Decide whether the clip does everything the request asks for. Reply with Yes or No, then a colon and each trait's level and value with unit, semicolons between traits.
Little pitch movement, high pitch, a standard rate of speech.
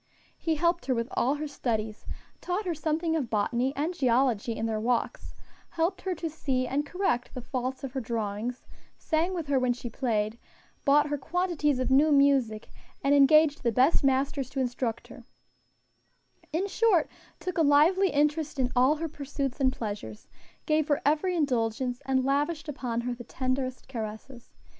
No: average, 4.0 semitones; very high, 275 Hz; average, 170 wpm